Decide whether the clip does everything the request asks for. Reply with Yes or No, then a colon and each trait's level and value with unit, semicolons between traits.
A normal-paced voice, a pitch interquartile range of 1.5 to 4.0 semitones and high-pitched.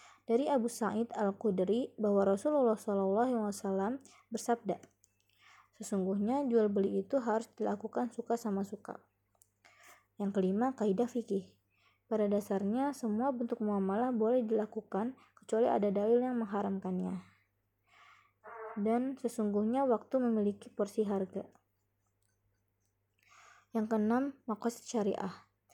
Yes: average, 105 wpm; average, 3.3 semitones; high, 215 Hz